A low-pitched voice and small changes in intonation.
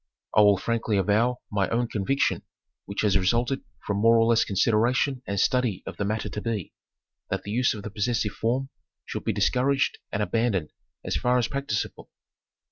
No: low, 115 Hz; average, 3.2 semitones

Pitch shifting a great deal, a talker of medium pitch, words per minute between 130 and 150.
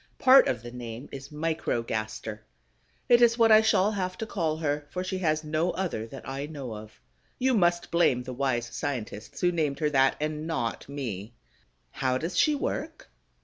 No: wide, 6.2 semitones; medium, 150 Hz; average, 185 wpm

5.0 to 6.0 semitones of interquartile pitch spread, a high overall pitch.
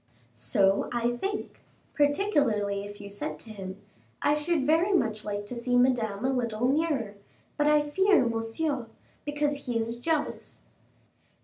Yes: wide, 5.6 semitones; high, 245 Hz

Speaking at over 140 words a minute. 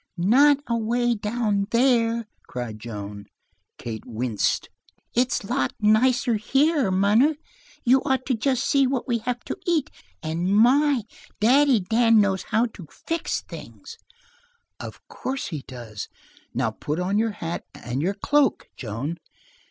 No: slow, 135 wpm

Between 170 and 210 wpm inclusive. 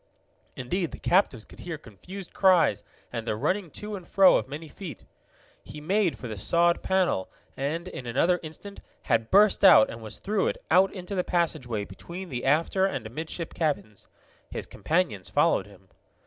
Yes: average, 175 wpm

